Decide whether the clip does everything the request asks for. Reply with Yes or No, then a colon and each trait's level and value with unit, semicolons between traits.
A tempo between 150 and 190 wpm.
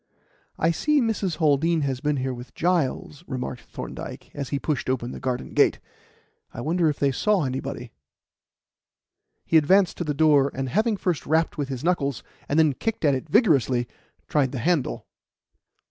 Yes: average, 170 wpm